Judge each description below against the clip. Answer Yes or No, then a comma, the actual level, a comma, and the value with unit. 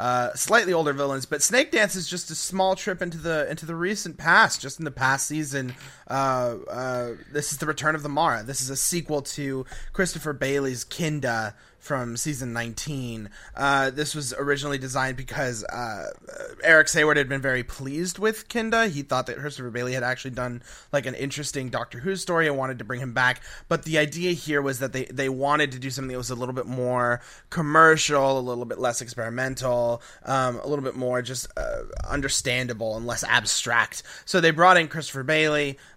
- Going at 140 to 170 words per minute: No, average, 200 wpm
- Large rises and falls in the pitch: No, average, 3.4 semitones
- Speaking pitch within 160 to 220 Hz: No, low, 135 Hz